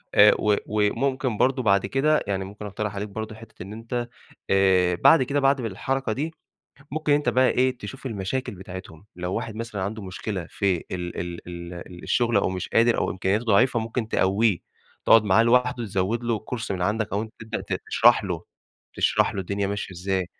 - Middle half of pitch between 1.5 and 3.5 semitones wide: No, average, 4.1 semitones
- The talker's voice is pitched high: No, low, 105 Hz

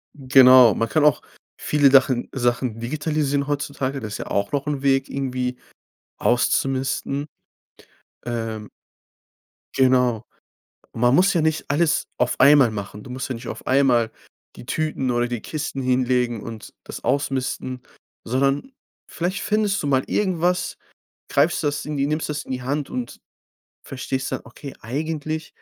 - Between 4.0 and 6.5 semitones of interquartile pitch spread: No, average, 3.0 semitones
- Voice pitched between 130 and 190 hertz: Yes, low, 135 Hz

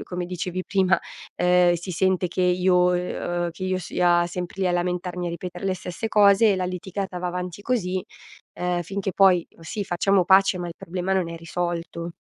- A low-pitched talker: No, medium, 180 Hz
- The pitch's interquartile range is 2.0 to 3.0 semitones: No, narrow, 1.3 semitones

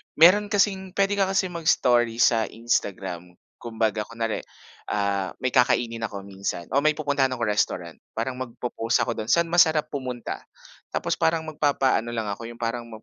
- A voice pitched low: Yes, low, 120 Hz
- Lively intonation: Yes, wide, 5.9 semitones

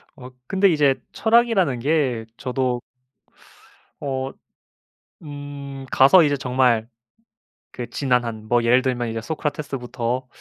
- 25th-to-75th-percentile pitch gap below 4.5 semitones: Yes, average, 2.9 semitones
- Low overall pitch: Yes, low, 130 Hz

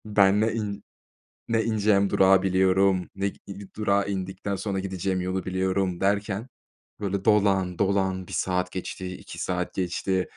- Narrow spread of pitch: Yes, narrow, 1.3 semitones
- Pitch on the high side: No, very low, 95 Hz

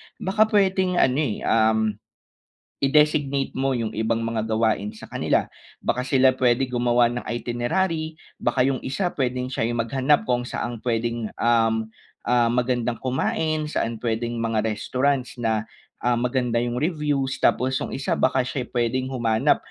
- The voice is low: Yes, low, 125 Hz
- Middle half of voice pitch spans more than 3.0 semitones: No, average, 2.7 semitones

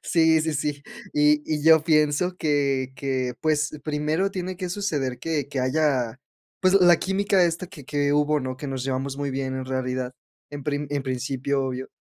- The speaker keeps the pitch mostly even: No, average, 3.2 semitones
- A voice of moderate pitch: Yes, medium, 145 Hz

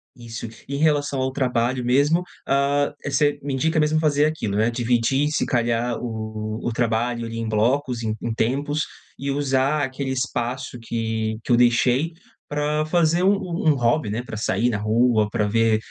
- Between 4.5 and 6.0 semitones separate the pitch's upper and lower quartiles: No, average, 3.8 semitones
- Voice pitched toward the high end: No, low, 125 Hz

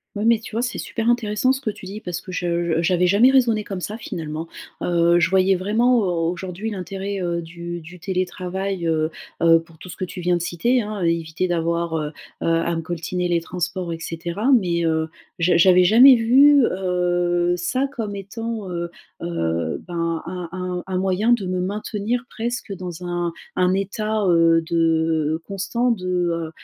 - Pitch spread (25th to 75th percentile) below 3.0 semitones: No, average, 3.5 semitones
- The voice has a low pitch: No, medium, 180 Hz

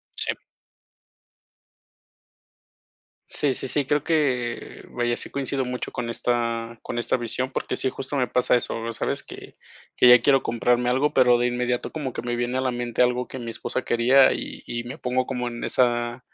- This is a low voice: Yes, low, 125 Hz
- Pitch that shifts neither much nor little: No, narrow, 1.5 semitones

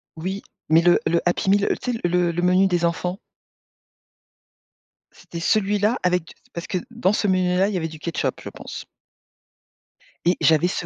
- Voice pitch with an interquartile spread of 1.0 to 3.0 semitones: Yes, narrow, 2.4 semitones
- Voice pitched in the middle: Yes, medium, 180 Hz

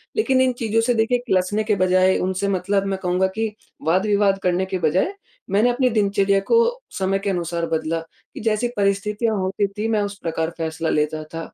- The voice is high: Yes, high, 195 Hz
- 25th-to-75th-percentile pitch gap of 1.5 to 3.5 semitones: Yes, average, 2.8 semitones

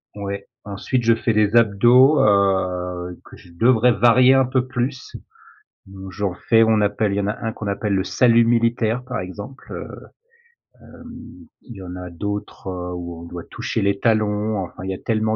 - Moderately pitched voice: No, low, 105 Hz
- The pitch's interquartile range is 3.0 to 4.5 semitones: Yes, average, 3.4 semitones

